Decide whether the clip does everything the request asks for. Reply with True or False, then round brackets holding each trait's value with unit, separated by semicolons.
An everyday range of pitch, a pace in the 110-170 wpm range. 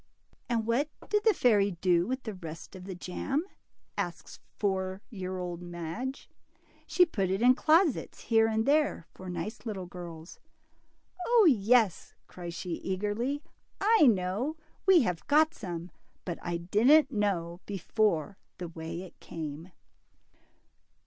False (5.8 semitones; 140 wpm)